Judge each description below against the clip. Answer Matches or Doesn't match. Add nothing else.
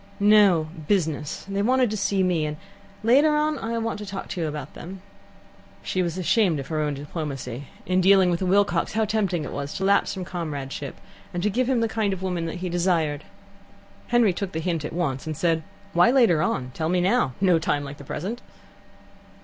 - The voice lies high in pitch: Doesn't match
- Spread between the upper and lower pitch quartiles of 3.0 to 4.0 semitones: Doesn't match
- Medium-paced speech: Doesn't match